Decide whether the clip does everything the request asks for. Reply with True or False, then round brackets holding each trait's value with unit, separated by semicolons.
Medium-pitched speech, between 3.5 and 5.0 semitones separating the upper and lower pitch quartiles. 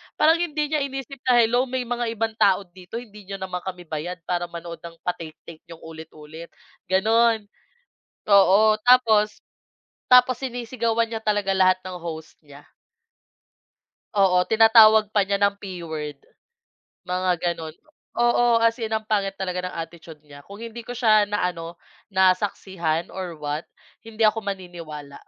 False (195 Hz; 4.7 semitones)